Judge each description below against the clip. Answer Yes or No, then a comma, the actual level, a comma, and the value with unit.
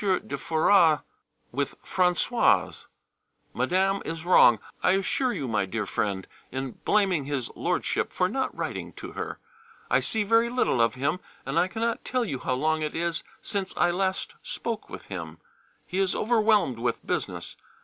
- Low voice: No, medium, 175 Hz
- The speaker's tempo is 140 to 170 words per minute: Yes, average, 160 wpm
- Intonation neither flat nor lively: No, wide, 7.1 semitones